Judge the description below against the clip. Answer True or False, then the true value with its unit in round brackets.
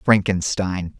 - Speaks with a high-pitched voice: False (95 Hz)